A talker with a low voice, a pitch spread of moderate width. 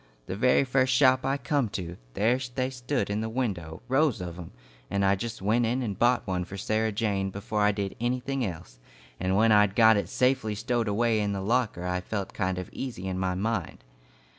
Yes: low, 105 Hz; average, 4.5 semitones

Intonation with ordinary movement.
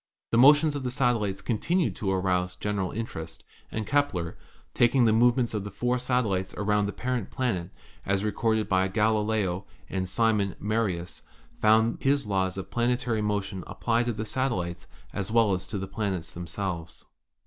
Yes: average, 3.9 semitones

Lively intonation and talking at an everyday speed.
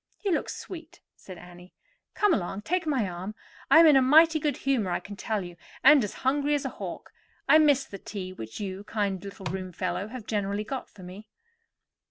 No: wide, 7.4 semitones; fast, 210 wpm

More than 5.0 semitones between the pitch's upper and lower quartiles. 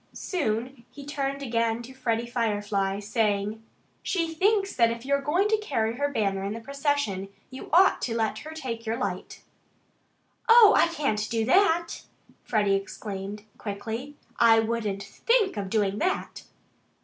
Yes: wide, 5.4 semitones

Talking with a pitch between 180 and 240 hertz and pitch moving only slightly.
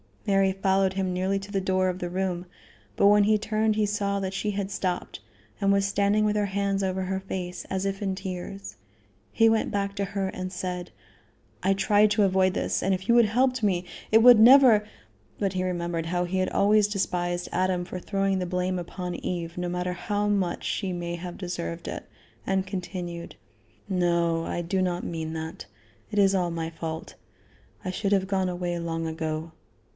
Yes: high, 190 Hz; narrow, 2.1 semitones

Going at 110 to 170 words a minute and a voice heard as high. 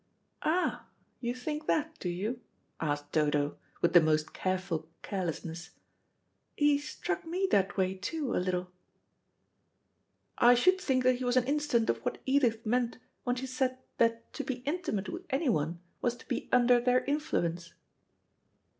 Yes: average, 150 wpm; high, 240 Hz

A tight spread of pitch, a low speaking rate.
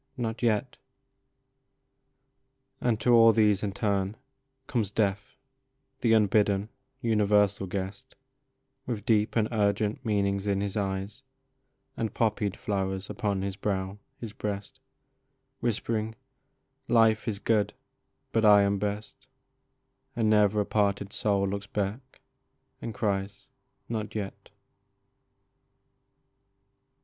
Yes: narrow, 1.8 semitones; slow, 120 wpm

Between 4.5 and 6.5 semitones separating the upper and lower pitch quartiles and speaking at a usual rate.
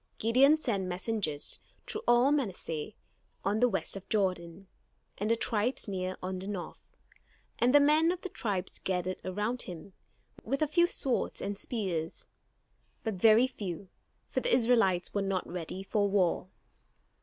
Yes: average, 4.8 semitones; average, 155 wpm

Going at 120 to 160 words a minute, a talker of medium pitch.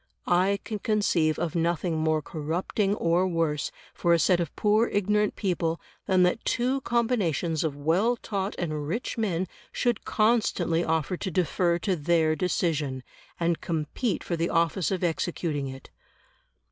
Yes: average, 150 wpm; medium, 175 Hz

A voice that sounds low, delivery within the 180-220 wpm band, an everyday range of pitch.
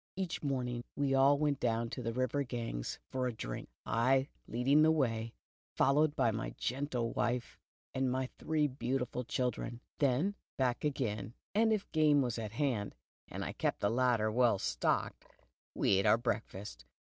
No: low, 125 Hz; average, 170 wpm; average, 3.5 semitones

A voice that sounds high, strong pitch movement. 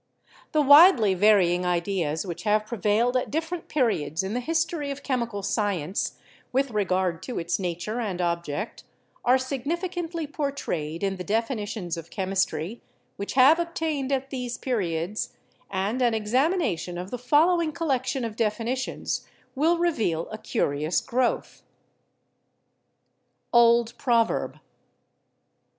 Yes: high, 230 Hz; wide, 6.6 semitones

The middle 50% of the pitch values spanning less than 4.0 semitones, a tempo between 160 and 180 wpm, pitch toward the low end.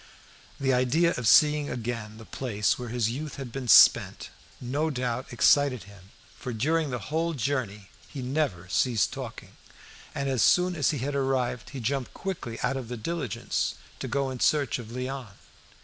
Yes: average, 3.4 semitones; average, 175 wpm; low, 130 Hz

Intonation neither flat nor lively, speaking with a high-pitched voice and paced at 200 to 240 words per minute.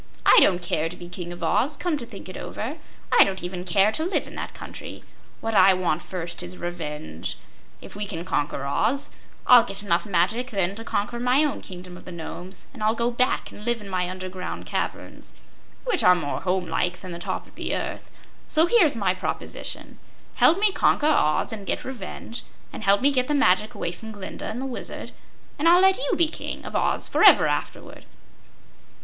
No: wide, 5.9 semitones; high, 195 Hz; fast, 205 wpm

